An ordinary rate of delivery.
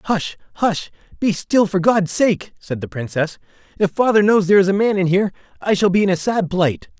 No: fast, 225 wpm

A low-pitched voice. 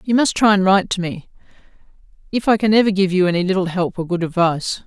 No: high, 190 Hz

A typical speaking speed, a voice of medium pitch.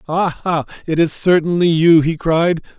Yes: average, 150 wpm; medium, 165 Hz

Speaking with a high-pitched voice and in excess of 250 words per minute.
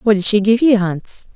Yes: high, 210 Hz; fast, 265 wpm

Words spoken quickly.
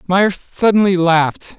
No: slow, 115 wpm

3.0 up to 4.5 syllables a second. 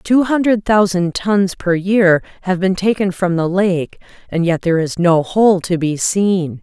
Yes: 4.1 syllables/s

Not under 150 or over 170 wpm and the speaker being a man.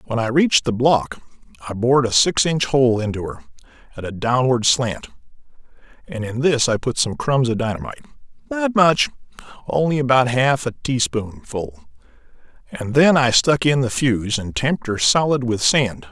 Yes: average, 165 wpm; male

